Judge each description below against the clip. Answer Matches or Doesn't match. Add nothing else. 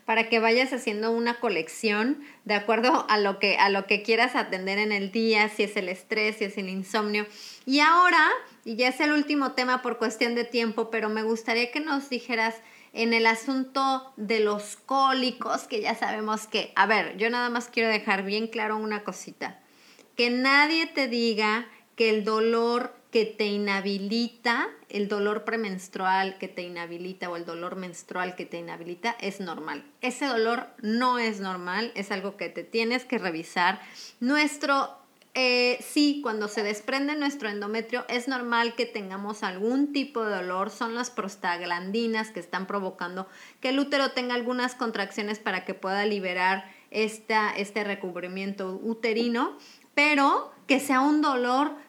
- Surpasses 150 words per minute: Matches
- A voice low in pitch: Doesn't match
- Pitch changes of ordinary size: Matches